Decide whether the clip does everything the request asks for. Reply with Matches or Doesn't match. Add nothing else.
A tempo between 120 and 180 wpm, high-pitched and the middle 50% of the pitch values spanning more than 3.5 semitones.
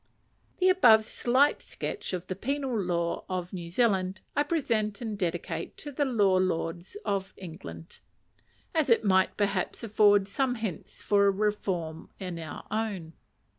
Matches